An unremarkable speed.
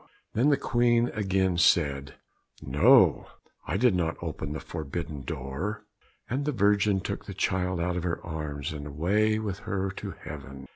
Yes: average, 160 wpm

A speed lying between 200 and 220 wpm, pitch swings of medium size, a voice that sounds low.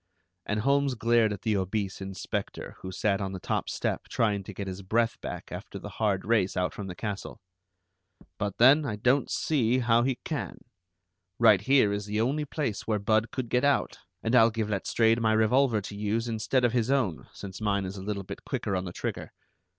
Yes: fast, 205 wpm; average, 3.1 semitones; low, 110 Hz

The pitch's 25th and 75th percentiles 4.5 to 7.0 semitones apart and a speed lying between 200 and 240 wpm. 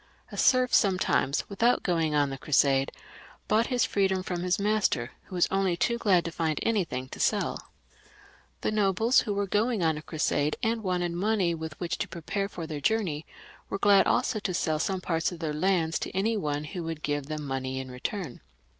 Yes: average, 4.8 semitones; fast, 205 wpm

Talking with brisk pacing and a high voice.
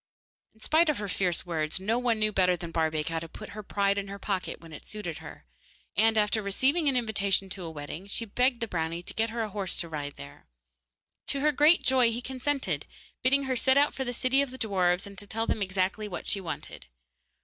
Yes: fast, 235 wpm; high, 205 Hz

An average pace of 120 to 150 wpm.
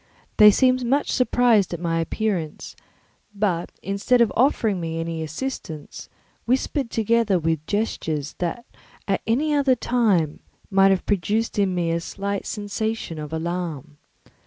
Yes: slow, 135 wpm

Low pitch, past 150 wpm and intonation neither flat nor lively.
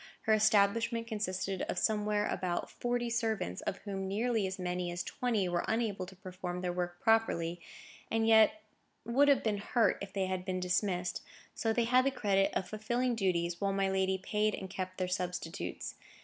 No: high, 195 Hz; average, 180 wpm; average, 3.4 semitones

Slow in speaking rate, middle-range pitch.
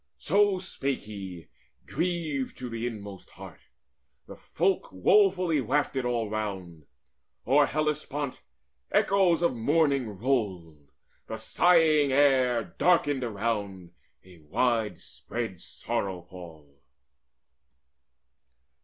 No: slow, 95 wpm; low, 120 Hz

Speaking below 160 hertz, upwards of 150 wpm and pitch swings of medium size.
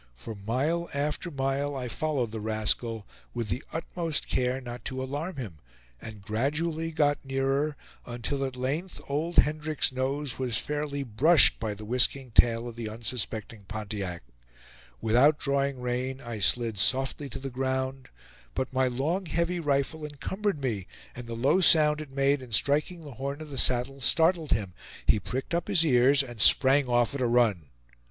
Yes: low, 135 Hz; average, 170 wpm; average, 3.8 semitones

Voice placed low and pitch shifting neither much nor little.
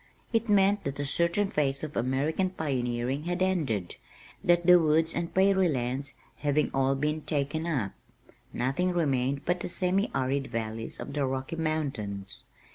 No: medium, 150 Hz; average, 4.7 semitones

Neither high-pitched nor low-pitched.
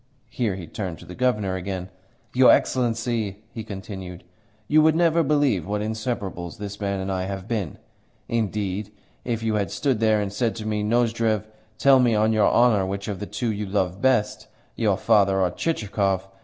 No: low, 105 Hz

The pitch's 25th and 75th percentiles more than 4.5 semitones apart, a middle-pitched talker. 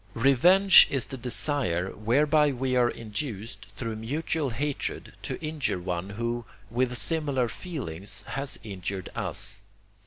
No: average, 5.1 semitones; low, 125 Hz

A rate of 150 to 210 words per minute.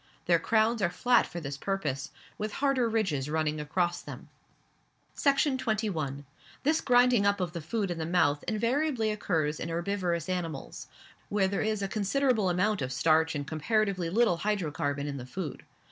Yes: average, 165 wpm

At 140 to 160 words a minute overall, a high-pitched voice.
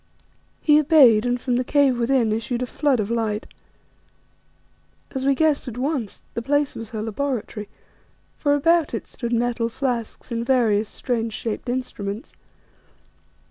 Yes: average, 145 wpm; high, 245 Hz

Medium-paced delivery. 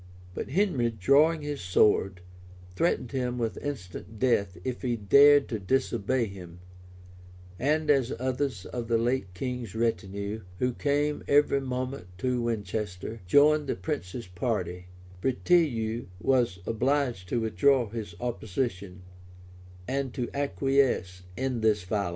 No: slow, 125 wpm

